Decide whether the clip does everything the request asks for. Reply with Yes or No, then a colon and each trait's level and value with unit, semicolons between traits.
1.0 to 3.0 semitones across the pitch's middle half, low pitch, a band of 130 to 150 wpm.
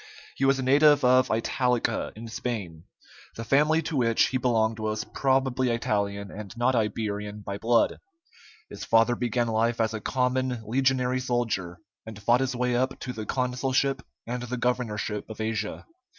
No: average, 2.7 semitones; low, 120 Hz; average, 165 wpm